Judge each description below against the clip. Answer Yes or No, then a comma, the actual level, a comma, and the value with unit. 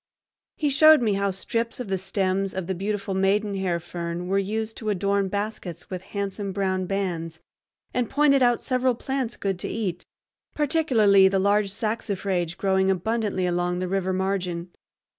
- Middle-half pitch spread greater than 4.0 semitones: No, average, 2.7 semitones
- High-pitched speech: Yes, high, 195 Hz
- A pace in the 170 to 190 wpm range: No, average, 160 wpm